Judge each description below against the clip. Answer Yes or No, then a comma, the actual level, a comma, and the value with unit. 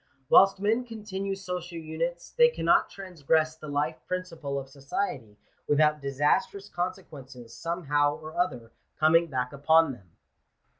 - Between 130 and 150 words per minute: Yes, average, 145 wpm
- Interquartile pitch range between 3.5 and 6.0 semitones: Yes, average, 4.6 semitones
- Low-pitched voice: No, medium, 160 Hz